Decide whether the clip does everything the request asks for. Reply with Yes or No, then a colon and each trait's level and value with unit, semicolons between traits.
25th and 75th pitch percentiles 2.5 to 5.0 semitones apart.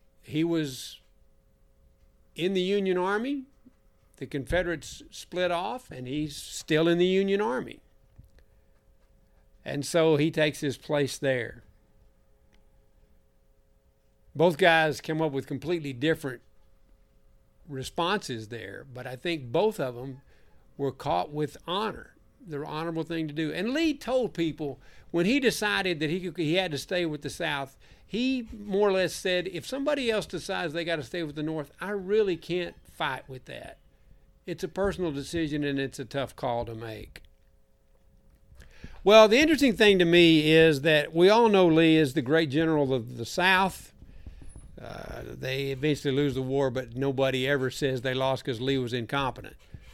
No: wide, 5.4 semitones